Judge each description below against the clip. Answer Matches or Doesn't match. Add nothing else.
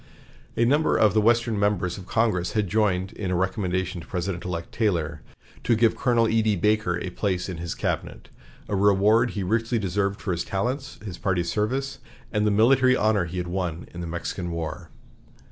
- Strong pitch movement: Doesn't match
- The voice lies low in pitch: Matches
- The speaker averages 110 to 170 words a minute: Doesn't match